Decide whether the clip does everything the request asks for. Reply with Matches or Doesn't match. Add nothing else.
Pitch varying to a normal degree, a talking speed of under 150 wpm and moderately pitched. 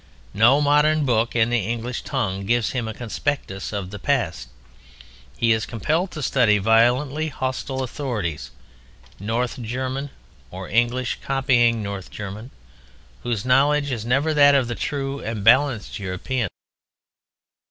Doesn't match